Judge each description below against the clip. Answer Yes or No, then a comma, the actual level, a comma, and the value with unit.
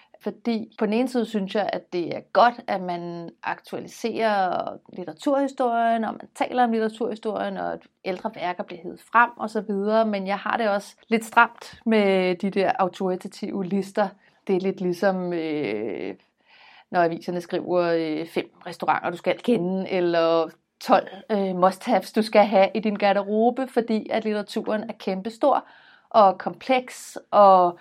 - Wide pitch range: No, average, 3.5 semitones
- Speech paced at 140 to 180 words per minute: Yes, average, 160 wpm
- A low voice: No, high, 200 Hz